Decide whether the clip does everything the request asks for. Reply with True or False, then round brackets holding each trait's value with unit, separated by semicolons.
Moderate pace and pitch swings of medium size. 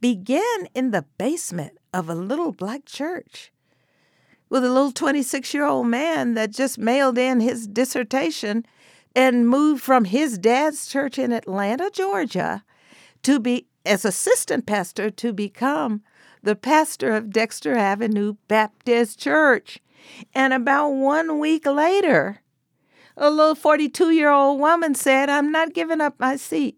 True (145 wpm; 4.7 semitones)